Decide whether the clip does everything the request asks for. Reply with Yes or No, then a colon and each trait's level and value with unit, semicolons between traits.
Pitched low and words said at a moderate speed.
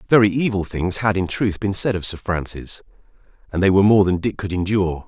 No: very low, 95 Hz; fast, 225 wpm